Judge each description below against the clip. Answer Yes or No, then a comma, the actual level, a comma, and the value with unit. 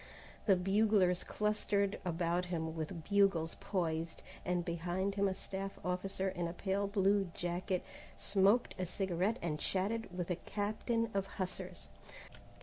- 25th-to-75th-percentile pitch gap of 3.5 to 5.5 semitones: No, narrow, 2.4 semitones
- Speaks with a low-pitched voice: No, high, 190 Hz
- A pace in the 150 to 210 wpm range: No, average, 140 wpm